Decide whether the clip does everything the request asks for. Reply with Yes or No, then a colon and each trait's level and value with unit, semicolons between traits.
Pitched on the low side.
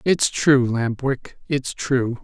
Yes: low, 130 Hz